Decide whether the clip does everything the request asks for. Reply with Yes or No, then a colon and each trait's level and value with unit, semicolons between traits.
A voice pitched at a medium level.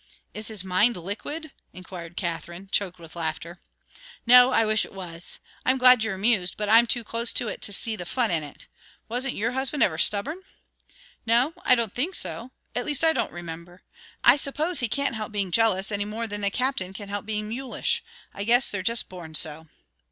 No: high, 215 Hz